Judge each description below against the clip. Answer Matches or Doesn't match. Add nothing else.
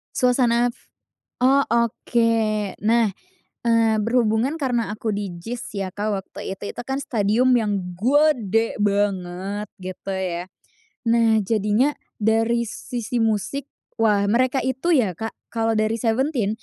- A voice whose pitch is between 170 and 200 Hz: Doesn't match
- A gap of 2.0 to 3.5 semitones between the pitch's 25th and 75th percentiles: Matches